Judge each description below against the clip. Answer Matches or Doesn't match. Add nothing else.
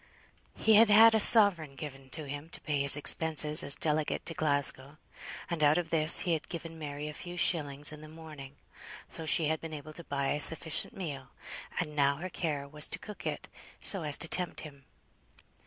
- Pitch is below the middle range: Doesn't match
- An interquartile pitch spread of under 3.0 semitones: Matches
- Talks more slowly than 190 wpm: Doesn't match